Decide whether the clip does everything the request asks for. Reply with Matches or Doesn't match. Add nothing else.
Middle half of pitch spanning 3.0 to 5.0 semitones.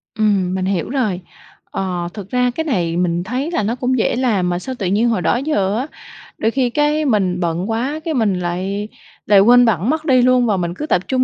Doesn't match